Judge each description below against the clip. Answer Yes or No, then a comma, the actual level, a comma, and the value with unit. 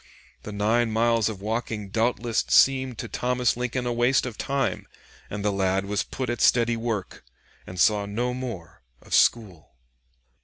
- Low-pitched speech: Yes, low, 115 Hz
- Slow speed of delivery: No, average, 160 wpm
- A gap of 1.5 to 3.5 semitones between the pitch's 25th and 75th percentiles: Yes, average, 3.1 semitones